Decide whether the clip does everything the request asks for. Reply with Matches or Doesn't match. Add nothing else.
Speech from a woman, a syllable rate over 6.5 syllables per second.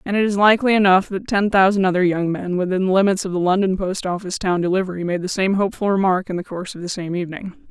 Matches